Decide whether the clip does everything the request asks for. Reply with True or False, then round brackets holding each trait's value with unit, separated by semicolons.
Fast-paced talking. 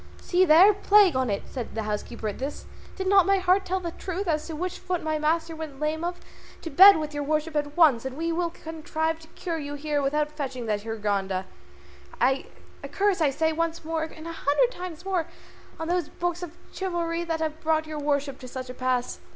True (215 wpm)